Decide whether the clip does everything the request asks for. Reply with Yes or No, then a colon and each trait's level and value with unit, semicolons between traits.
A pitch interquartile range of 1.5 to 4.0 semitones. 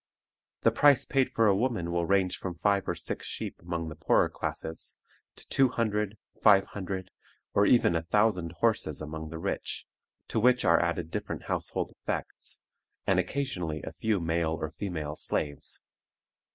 No: average, 4.5 semitones